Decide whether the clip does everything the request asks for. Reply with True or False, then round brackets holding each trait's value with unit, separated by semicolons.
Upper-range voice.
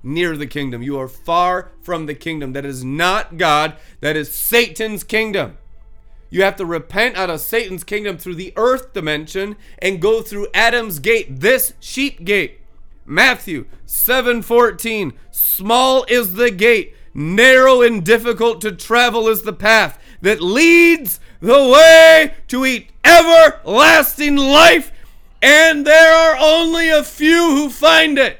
True (225 Hz)